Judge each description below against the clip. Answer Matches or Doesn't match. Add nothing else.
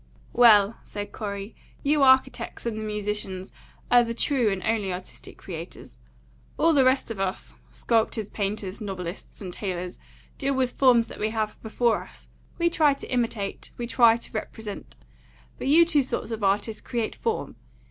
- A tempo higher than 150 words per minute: Matches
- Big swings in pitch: Doesn't match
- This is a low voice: Doesn't match